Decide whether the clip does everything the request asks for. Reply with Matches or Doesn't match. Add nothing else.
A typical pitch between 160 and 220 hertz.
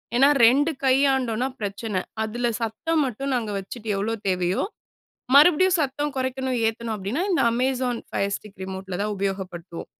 Doesn't match